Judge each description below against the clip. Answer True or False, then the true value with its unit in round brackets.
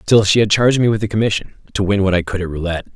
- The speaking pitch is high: False (100 Hz)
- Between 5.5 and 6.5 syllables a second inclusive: False (7.4 syllables/s)